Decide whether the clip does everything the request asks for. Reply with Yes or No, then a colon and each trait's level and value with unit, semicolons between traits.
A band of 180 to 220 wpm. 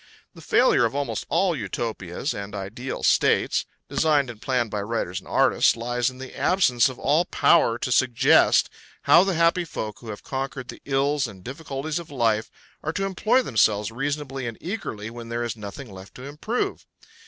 Yes: average, 185 wpm